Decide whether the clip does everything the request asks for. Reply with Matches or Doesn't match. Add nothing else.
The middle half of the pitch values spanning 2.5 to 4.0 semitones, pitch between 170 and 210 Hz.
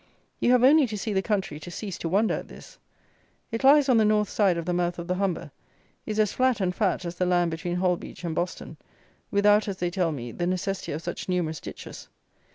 Matches